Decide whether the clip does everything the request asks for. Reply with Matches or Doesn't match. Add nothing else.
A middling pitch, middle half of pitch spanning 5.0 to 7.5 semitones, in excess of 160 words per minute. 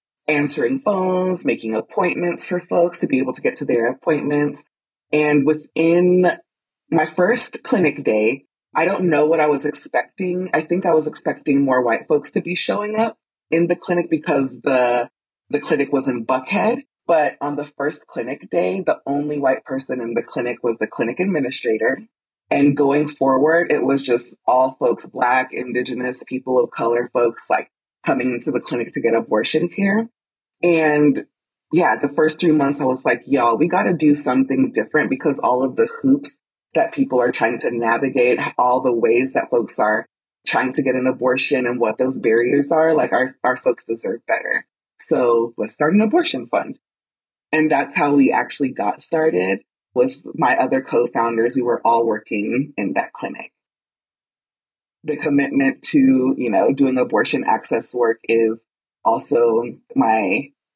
Matches